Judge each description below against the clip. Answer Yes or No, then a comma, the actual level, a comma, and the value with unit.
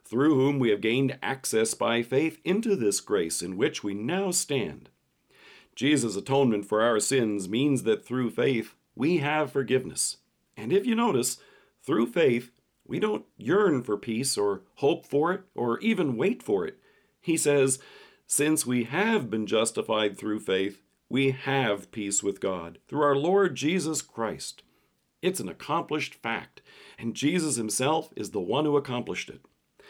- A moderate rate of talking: Yes, average, 160 wpm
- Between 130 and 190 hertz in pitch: Yes, low, 135 Hz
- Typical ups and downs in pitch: No, wide, 6.0 semitones